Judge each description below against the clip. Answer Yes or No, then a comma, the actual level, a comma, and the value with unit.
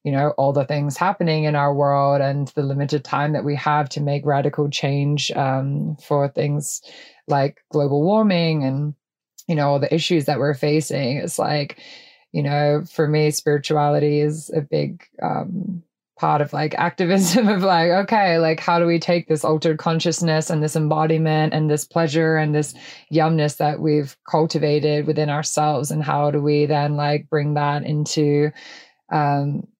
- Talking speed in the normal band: Yes, average, 170 wpm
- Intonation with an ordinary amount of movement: No, narrow, 1.6 semitones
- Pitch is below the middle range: No, medium, 150 Hz